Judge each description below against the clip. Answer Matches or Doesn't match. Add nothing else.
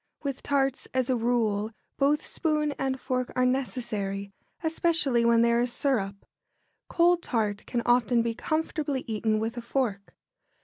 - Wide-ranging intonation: Doesn't match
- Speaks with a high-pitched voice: Matches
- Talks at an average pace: Matches